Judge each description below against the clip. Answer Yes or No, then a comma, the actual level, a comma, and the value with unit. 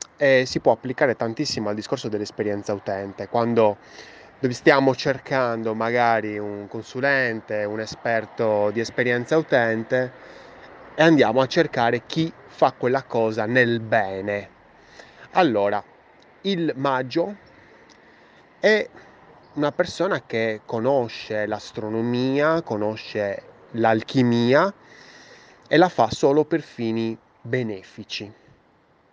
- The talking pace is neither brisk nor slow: No, slow, 100 wpm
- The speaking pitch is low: Yes, low, 115 Hz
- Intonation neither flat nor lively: Yes, average, 3.6 semitones